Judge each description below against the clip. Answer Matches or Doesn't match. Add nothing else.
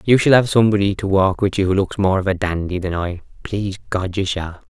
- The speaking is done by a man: Matches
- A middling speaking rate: Doesn't match